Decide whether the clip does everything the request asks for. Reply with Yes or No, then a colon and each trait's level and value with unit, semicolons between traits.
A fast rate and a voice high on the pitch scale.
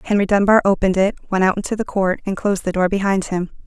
Yes: fast, 245 wpm; high, 195 Hz